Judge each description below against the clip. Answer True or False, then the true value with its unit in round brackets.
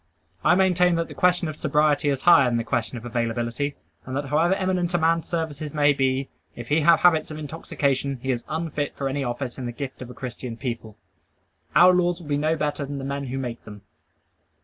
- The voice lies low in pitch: False (145 Hz)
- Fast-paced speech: True (220 wpm)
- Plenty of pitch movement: False (4.1 semitones)